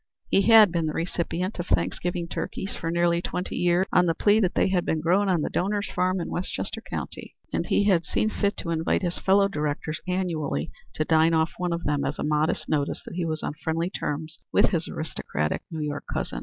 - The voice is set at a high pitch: No, medium, 170 Hz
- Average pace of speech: No, fast, 220 wpm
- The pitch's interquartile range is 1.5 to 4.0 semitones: Yes, average, 2.8 semitones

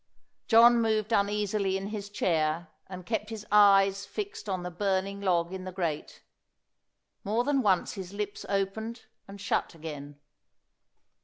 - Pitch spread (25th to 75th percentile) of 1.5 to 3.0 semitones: Yes, narrow, 2.6 semitones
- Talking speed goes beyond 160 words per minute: No, average, 145 wpm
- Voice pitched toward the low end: No, high, 200 Hz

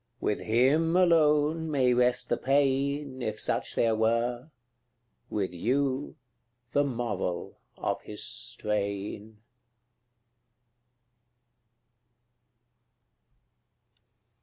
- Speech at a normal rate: No, slow, 75 wpm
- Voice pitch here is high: No, low, 125 Hz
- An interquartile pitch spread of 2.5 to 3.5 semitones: No, average, 4.5 semitones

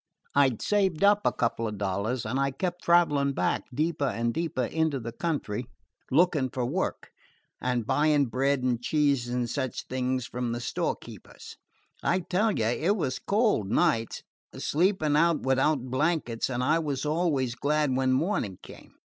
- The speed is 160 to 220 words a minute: Yes, average, 165 wpm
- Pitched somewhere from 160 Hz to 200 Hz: No, low, 135 Hz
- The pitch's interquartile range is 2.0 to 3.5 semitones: No, average, 4.6 semitones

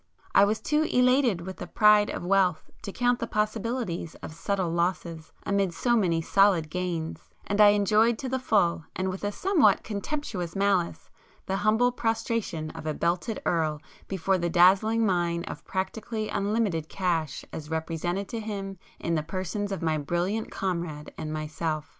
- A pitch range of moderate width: Yes, average, 4.1 semitones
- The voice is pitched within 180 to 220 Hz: Yes, high, 190 Hz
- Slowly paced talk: No, average, 165 wpm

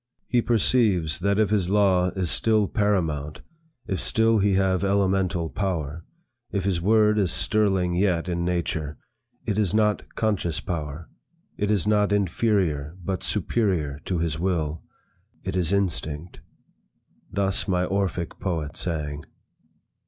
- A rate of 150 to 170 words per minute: No, slow, 135 wpm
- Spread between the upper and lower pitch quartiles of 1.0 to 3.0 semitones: No, average, 3.6 semitones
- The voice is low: Yes, very low, 95 Hz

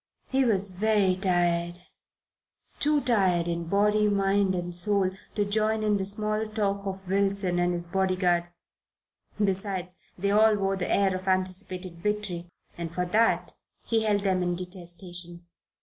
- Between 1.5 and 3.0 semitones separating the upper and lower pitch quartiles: Yes, narrow, 2.6 semitones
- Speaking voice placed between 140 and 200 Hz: Yes, high, 190 Hz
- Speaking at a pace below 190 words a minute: Yes, average, 150 wpm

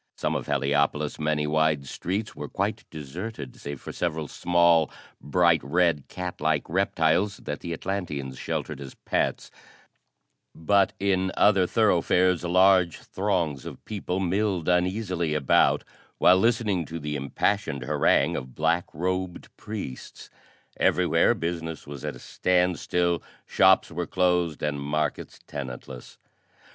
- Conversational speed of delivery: No, slow, 130 wpm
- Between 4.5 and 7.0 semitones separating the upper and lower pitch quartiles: No, average, 3.7 semitones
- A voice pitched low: Yes, very low, 85 Hz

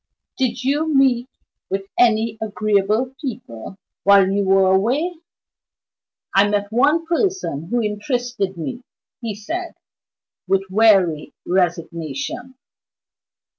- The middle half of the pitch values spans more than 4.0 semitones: Yes, average, 5.0 semitones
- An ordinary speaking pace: No, slow, 100 wpm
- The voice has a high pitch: Yes, high, 215 Hz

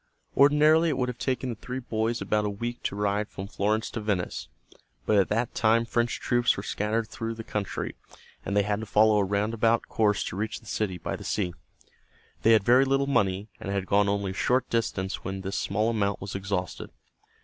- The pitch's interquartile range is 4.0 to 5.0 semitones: No, average, 2.8 semitones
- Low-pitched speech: Yes, low, 105 Hz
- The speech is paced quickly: Yes, fast, 210 wpm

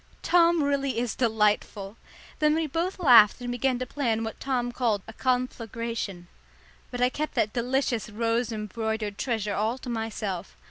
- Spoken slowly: No, average, 155 wpm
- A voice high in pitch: Yes, high, 235 Hz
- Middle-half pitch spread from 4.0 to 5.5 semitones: No, average, 3.1 semitones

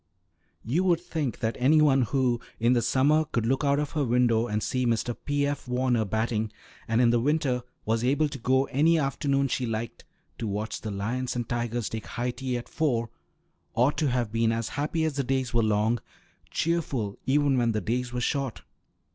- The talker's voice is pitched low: Yes, low, 125 Hz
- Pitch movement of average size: Yes, average, 3.4 semitones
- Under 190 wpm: No, average, 200 wpm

